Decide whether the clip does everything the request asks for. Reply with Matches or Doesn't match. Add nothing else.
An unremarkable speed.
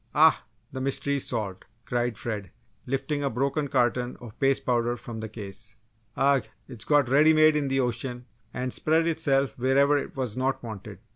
Matches